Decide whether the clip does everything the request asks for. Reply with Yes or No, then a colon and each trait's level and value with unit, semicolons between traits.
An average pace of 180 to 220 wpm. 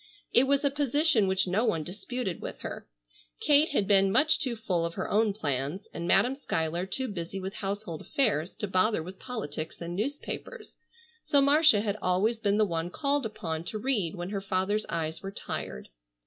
Yes: average, 190 wpm